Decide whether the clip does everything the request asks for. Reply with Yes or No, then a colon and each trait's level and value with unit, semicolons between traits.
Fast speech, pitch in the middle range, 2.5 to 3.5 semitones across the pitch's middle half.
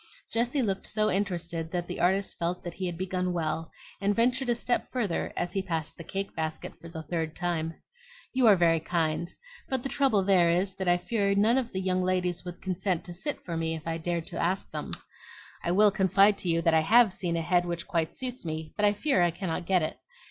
Yes: fast, 235 wpm; medium, 180 Hz; average, 3.1 semitones